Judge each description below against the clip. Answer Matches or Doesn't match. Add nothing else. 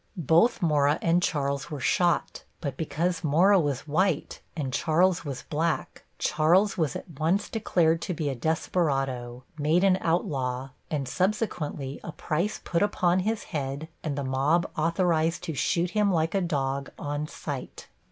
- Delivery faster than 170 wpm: Doesn't match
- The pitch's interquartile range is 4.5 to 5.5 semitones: Doesn't match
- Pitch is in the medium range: Matches